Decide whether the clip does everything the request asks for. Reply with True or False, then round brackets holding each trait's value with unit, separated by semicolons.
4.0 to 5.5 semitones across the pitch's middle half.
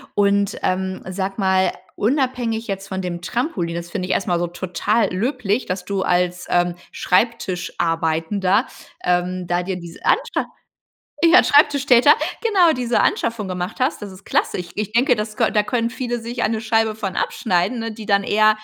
True (4.3 semitones)